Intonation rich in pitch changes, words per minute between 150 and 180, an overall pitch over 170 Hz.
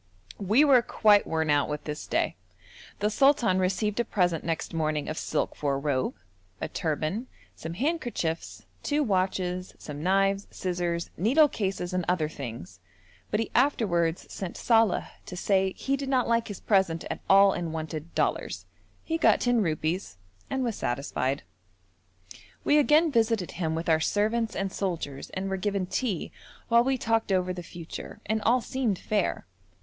Yes: wide, 5.8 semitones; average, 165 wpm; high, 190 Hz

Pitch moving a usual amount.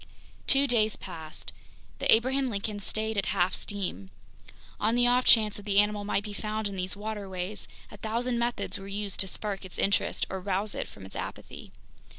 No: narrow, 2.2 semitones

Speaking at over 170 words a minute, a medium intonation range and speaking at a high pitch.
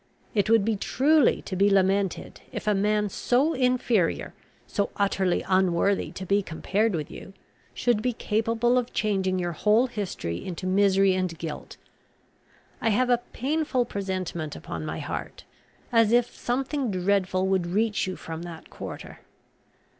No: average, 150 wpm; average, 3.7 semitones; high, 200 Hz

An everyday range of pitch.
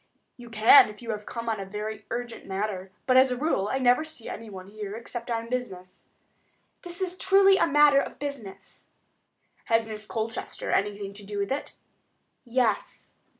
Yes: average, 3.8 semitones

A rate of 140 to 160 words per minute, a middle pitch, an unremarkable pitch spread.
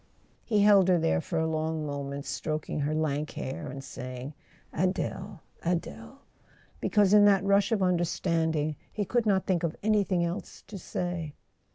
Yes: average, 155 wpm; medium, 170 Hz; average, 4.4 semitones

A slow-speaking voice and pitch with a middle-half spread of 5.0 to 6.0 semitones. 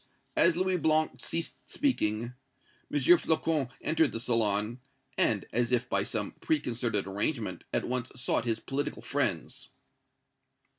Yes: slow, 130 wpm; wide, 5.6 semitones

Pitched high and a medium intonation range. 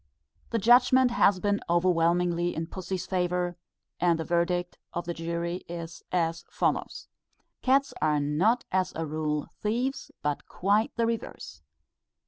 No: medium, 175 Hz; average, 3.5 semitones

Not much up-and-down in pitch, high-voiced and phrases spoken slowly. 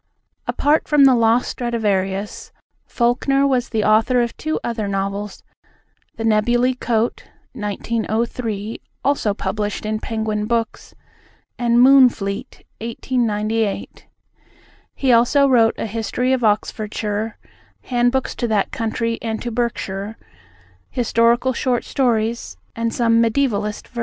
Yes: narrow, 2.3 semitones; high, 230 Hz; slow, 115 wpm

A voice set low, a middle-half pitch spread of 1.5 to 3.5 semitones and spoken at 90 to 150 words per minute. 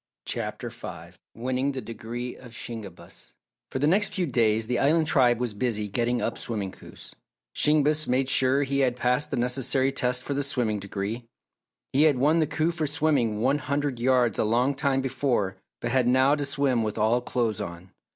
No: low, 125 Hz; average, 3.2 semitones; average, 190 wpm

